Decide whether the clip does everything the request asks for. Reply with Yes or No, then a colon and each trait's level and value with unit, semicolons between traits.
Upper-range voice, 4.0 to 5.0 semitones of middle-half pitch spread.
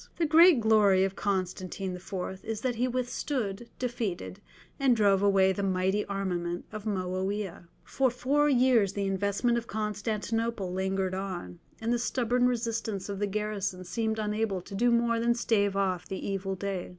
No: high, 205 Hz; average, 3.5 semitones